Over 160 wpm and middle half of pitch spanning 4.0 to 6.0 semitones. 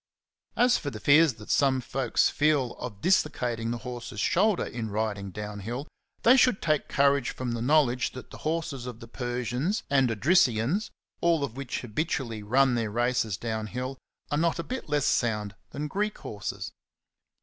Yes: average, 170 wpm; average, 4.8 semitones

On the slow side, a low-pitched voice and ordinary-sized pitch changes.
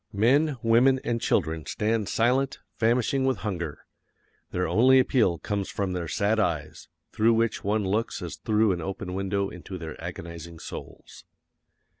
No: average, 150 wpm; low, 105 Hz; average, 4.5 semitones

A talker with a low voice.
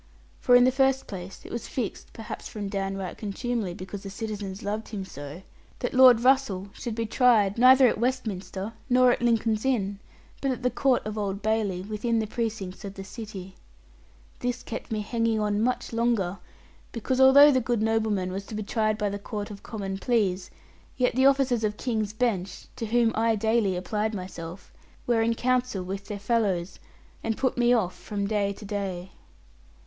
No: high, 215 Hz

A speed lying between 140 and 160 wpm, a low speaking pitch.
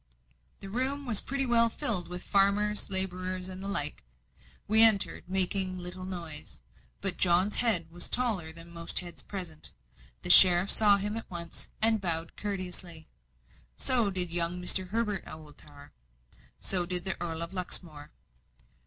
No: average, 150 wpm; medium, 185 Hz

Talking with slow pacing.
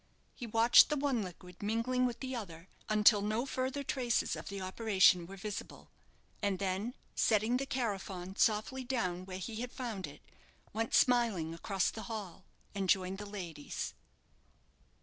No: average, 155 wpm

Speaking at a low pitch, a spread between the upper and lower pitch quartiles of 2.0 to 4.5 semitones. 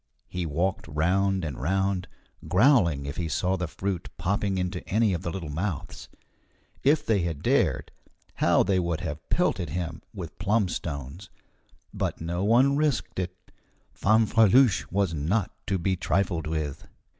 Yes: very low, 90 Hz; average, 3.3 semitones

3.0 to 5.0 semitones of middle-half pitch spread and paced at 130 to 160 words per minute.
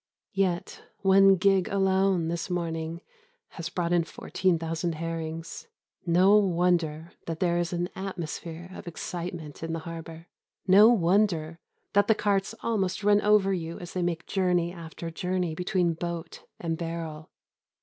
No: narrow, 2.5 semitones; average, 145 wpm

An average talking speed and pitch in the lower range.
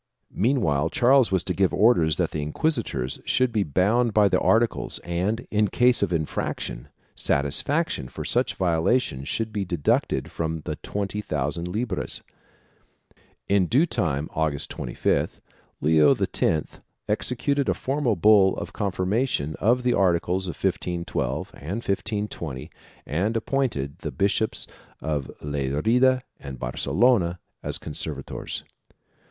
No: slow, 130 wpm; very low, 95 Hz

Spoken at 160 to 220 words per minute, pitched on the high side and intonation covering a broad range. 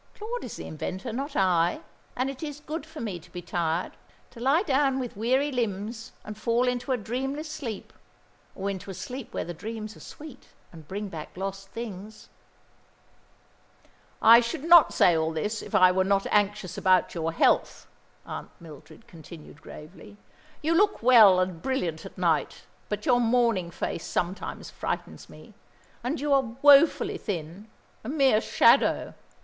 Yes: average, 165 wpm; high, 215 Hz; wide, 6.3 semitones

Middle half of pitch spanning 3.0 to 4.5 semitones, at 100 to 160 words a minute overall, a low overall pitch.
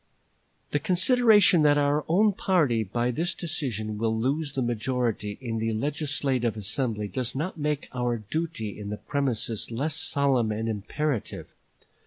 No: average, 5.1 semitones; average, 145 wpm; low, 130 Hz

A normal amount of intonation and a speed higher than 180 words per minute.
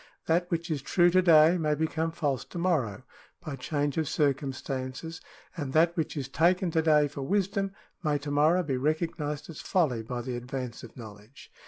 Yes: average, 3.8 semitones; average, 195 wpm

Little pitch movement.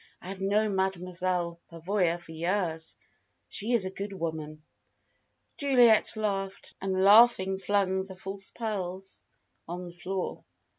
Yes: narrow, 2.3 semitones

